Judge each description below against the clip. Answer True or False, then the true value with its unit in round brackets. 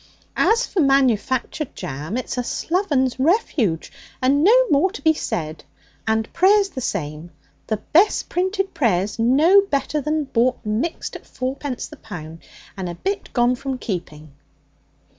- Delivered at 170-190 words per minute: False (150 wpm)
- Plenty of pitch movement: True (7.7 semitones)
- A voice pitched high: True (260 Hz)